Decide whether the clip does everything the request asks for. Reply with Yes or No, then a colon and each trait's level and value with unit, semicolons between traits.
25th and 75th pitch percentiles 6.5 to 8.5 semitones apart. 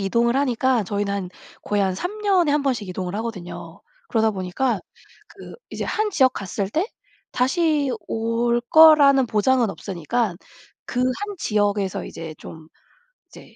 No: wide, 5.6 semitones